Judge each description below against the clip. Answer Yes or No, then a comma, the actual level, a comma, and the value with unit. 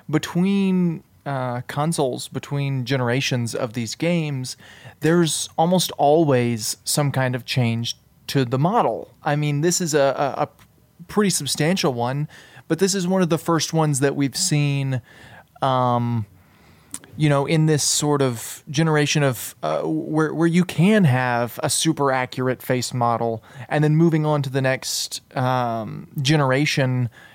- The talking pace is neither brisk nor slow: Yes, average, 150 wpm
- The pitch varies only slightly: No, average, 3.9 semitones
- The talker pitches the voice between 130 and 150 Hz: Yes, medium, 140 Hz